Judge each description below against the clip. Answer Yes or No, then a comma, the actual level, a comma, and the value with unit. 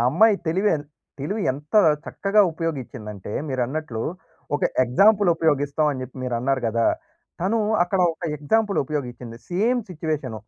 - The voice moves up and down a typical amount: No, wide, 6.7 semitones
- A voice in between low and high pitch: Yes, medium, 150 Hz